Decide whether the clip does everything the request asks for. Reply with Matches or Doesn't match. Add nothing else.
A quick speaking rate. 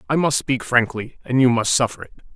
Matches